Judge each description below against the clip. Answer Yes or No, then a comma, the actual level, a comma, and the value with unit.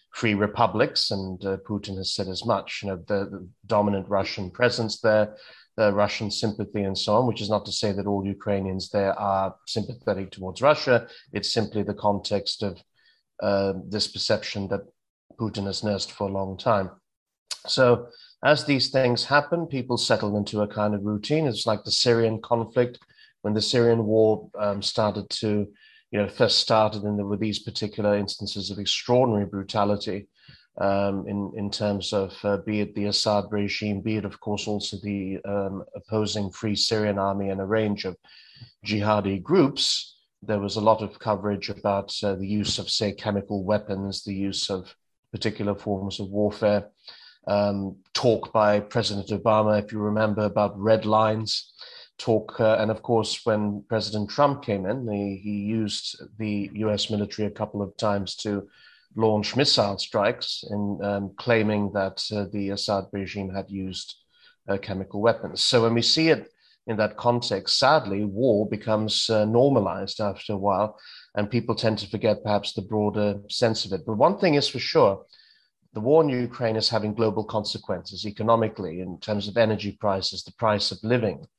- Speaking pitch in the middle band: No, low, 105 Hz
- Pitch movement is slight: Yes, narrow, 1.7 semitones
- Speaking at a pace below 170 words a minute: No, average, 175 wpm